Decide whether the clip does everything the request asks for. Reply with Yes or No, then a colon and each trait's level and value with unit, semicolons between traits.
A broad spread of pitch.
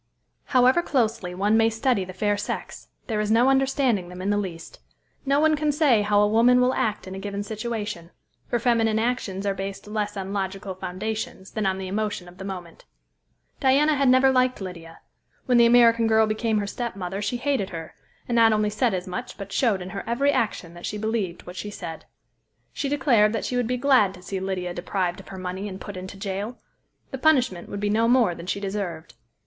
No: average, 4.0 semitones